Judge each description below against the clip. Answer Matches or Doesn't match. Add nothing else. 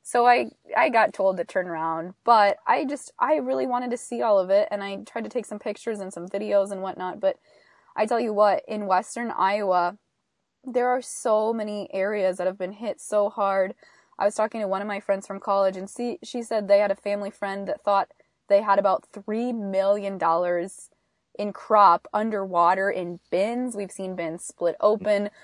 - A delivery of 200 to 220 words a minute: Matches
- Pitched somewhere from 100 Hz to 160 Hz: Doesn't match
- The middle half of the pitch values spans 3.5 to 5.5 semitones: Doesn't match